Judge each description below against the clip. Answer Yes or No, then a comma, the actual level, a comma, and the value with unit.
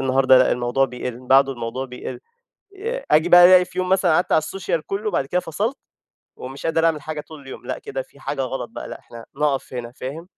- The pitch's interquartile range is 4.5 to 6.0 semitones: Yes, wide, 5.6 semitones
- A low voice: No, medium, 150 Hz